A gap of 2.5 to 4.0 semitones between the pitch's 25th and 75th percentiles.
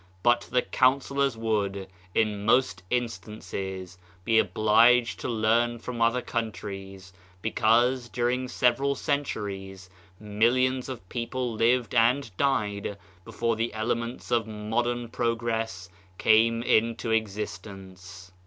Yes: average, 2.8 semitones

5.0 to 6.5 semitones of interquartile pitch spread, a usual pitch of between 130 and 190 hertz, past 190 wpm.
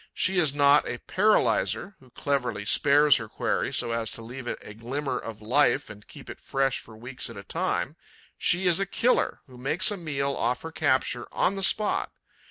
Yes: wide, 5.5 semitones; low, 135 Hz; average, 200 wpm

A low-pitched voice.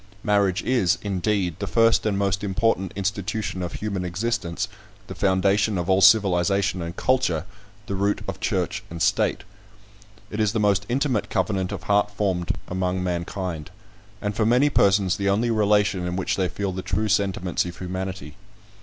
Yes: low, 100 Hz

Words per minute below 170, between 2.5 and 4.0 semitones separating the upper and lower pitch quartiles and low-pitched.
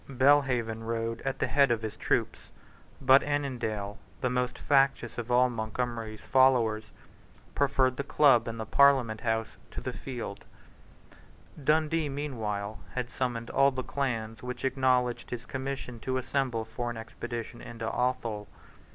Yes: average, 145 wpm; average, 2.9 semitones; low, 125 Hz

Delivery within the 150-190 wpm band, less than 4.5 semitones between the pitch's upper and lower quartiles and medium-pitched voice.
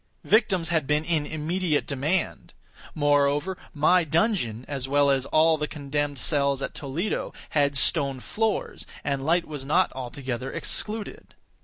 No: average, 140 wpm; average, 3.3 semitones; medium, 145 Hz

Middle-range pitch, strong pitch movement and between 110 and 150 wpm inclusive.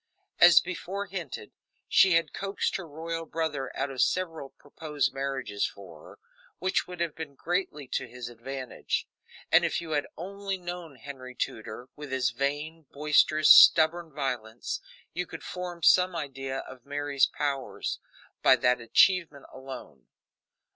No: medium, 145 Hz; average, 4.4 semitones; average, 145 wpm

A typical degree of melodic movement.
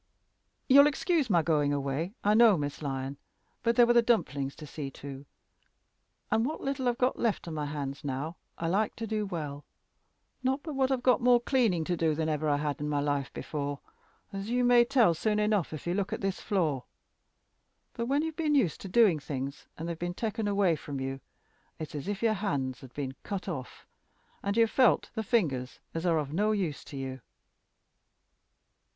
No: wide, 8.1 semitones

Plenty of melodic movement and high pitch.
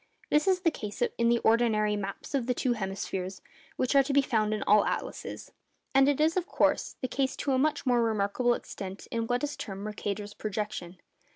No: average, 4.6 semitones; high, 230 Hz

